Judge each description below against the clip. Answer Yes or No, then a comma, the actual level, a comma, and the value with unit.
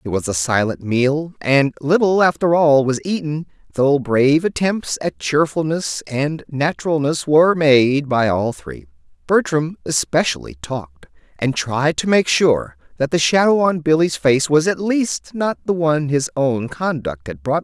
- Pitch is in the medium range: Yes, medium, 145 Hz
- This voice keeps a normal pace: Yes, average, 165 wpm